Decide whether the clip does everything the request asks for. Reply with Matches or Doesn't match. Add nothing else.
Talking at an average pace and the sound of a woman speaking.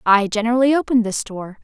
Matches